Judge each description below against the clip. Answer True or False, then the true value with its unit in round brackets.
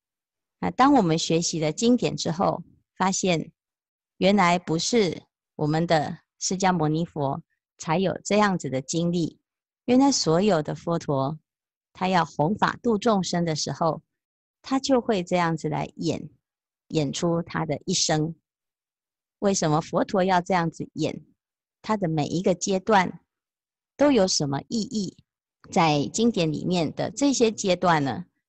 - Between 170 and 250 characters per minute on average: True (205 characters per minute)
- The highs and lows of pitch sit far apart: False (4.2 semitones)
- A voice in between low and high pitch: True (175 Hz)